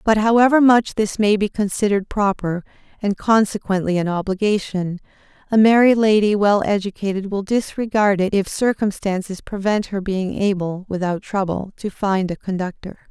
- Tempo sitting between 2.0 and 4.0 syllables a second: No, 5.0 syllables/s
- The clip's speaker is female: Yes, female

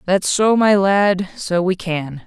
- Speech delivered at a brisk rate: No, average, 185 wpm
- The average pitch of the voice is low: No, high, 190 Hz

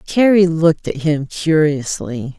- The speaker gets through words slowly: Yes, slow, 125 wpm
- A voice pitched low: No, medium, 160 Hz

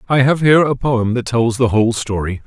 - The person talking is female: No, male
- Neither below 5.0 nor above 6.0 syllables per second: Yes, 5.8 syllables/s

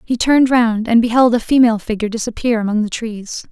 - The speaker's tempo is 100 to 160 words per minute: No, fast, 205 wpm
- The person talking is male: No, female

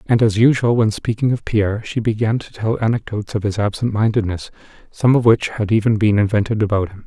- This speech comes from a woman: No, male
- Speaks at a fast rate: Yes, fast, 210 wpm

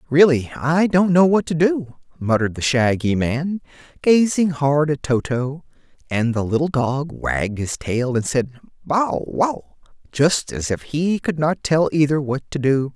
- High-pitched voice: No, medium, 145 Hz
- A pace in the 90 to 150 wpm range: No, average, 170 wpm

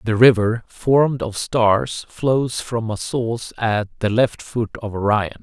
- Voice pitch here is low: Yes, low, 115 Hz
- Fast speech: No, average, 165 wpm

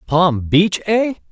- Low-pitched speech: No, medium, 180 Hz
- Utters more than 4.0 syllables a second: No, 3.1 syllables/s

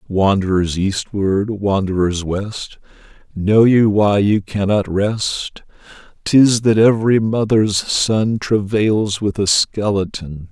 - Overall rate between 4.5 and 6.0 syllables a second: No, 3.3 syllables/s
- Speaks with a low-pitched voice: Yes, low, 100 Hz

